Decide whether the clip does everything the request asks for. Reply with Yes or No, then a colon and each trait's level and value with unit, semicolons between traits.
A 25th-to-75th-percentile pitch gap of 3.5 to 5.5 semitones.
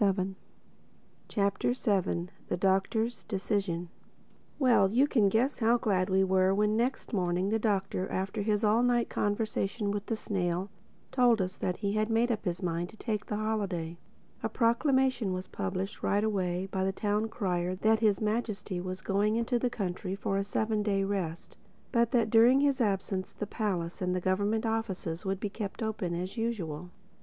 No: average, 3.0 semitones